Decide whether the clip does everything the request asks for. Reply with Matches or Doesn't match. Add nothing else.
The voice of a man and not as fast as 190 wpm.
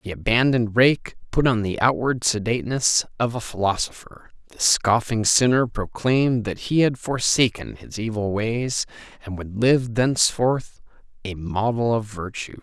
Matches